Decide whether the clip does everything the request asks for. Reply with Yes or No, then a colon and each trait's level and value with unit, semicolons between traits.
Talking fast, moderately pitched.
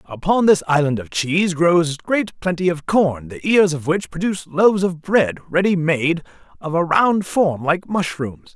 No: average, 180 wpm; medium, 170 Hz